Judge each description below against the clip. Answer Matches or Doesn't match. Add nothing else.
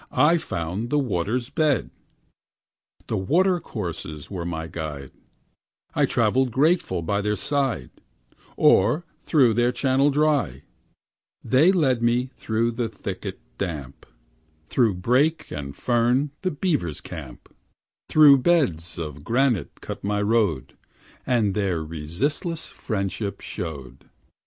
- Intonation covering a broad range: Matches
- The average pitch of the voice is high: Doesn't match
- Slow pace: Matches